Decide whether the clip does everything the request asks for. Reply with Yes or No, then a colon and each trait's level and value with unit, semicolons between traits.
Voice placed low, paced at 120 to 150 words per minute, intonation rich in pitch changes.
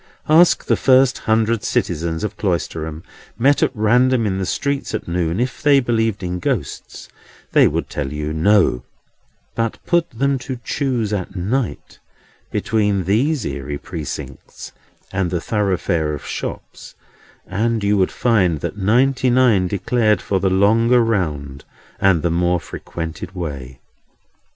Yes: low, 100 Hz; average, 140 wpm; wide, 5.8 semitones